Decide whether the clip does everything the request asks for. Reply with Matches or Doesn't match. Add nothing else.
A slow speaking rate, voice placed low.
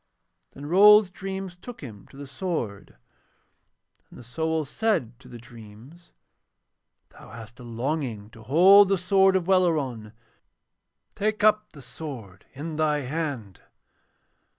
Doesn't match